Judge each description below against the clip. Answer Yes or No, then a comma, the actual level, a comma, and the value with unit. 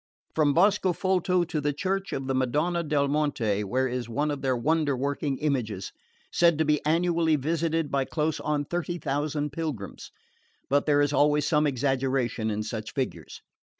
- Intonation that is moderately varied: Yes, average, 3.3 semitones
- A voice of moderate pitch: Yes, medium, 145 Hz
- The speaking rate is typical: Yes, average, 165 wpm